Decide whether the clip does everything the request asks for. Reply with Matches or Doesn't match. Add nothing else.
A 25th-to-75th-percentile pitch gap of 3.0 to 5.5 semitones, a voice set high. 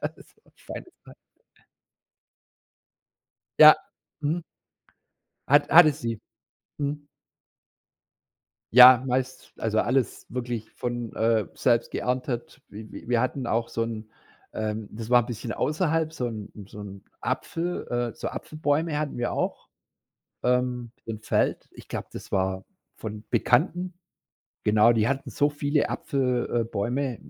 Doesn't match